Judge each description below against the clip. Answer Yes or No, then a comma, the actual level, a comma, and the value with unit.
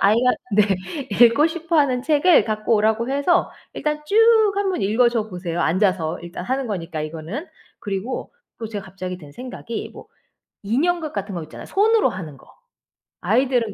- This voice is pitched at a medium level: No, high, 225 Hz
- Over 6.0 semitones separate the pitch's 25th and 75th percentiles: Yes, wide, 7.2 semitones